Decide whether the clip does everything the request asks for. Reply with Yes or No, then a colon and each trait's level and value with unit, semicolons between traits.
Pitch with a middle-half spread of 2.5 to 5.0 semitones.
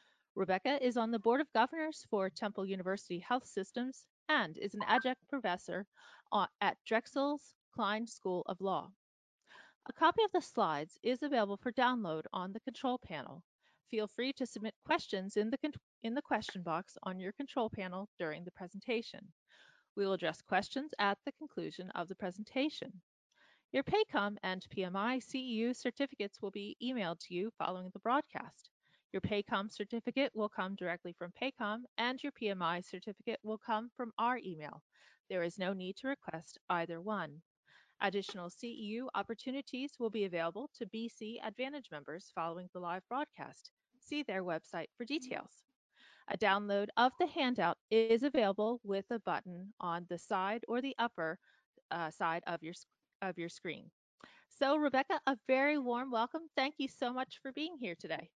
No: wide, 5.5 semitones